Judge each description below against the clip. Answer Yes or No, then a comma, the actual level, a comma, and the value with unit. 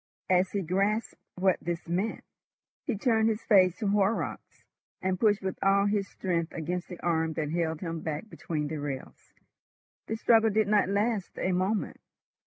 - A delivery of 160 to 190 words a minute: Yes, average, 170 wpm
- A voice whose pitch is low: No, high, 190 Hz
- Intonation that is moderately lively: Yes, average, 3.6 semitones